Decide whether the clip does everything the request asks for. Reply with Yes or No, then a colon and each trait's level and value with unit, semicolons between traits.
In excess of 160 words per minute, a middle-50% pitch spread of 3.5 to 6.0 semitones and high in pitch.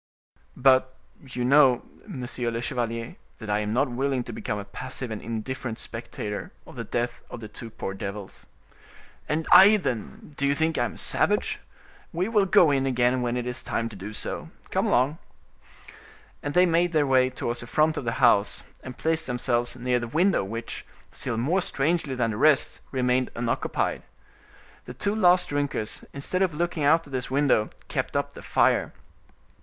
No: average, 180 wpm; average, 4.2 semitones; low, 130 Hz